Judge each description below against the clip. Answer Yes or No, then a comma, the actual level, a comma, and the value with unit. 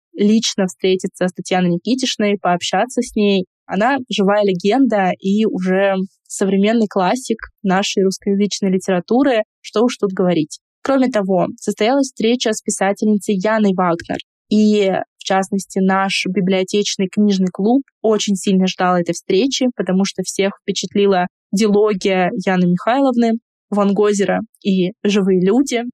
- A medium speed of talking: Yes, average, 125 wpm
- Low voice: No, high, 200 Hz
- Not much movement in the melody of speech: Yes, narrow, 2.3 semitones